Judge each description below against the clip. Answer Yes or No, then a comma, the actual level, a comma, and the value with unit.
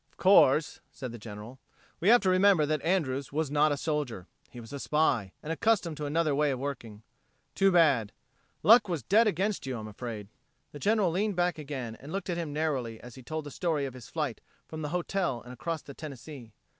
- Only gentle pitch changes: No, average, 5.3 semitones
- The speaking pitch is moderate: Yes, medium, 150 Hz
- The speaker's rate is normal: No, fast, 215 wpm